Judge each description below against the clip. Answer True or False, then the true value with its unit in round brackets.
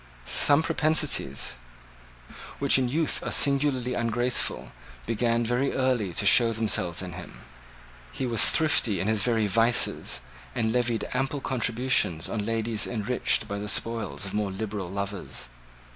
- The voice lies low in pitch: True (115 Hz)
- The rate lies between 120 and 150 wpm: True (140 wpm)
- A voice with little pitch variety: False (3.8 semitones)